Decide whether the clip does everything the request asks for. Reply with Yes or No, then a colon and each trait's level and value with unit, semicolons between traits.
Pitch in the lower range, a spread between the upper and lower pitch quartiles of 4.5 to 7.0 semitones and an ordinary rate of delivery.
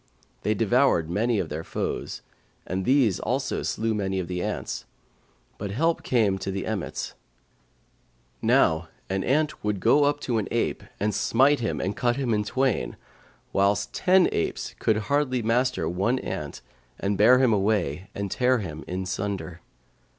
Yes: low, 105 Hz; average, 4.8 semitones; average, 160 wpm